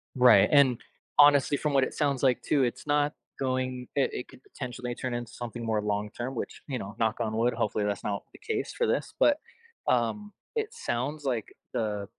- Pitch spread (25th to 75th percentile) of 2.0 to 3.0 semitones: No, average, 3.8 semitones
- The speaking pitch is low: Yes, low, 125 Hz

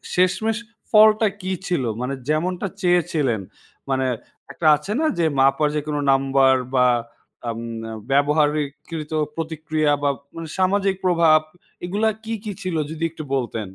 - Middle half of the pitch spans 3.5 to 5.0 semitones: Yes, average, 4.7 semitones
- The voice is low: No, medium, 155 Hz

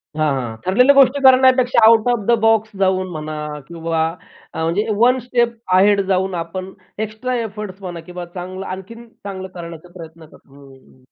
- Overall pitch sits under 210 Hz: Yes, high, 190 Hz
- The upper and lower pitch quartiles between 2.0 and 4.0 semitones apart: No, wide, 5.4 semitones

